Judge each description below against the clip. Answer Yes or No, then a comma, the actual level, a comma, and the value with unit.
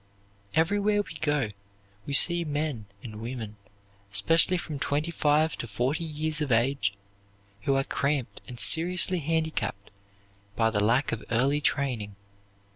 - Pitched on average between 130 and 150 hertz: Yes, medium, 140 Hz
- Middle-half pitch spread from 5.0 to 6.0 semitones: Yes, wide, 5.4 semitones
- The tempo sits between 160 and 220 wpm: No, slow, 135 wpm